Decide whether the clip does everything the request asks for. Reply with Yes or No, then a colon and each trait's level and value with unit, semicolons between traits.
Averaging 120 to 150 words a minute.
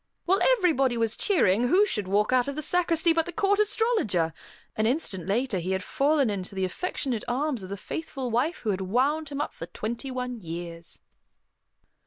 No: average, 190 wpm